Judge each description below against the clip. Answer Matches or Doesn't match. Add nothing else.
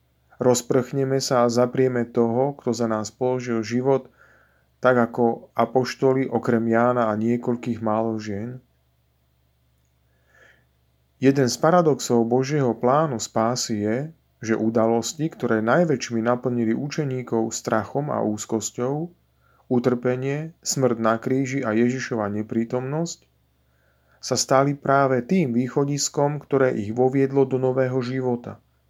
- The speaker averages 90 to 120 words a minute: Matches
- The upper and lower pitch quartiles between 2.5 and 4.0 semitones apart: Matches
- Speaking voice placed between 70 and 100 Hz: Doesn't match